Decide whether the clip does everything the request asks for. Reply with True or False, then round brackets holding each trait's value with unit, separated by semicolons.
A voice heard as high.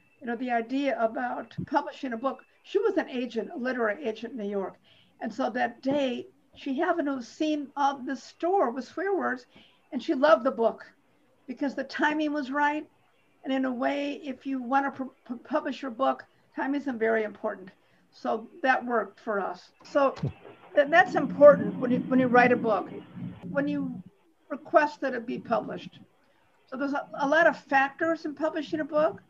True (275 Hz)